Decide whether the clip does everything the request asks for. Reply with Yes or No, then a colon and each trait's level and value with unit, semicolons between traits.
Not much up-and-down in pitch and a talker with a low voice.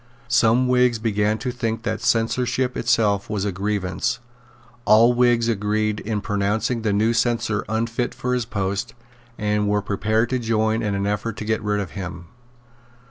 Yes: narrow, 2.2 semitones; low, 110 Hz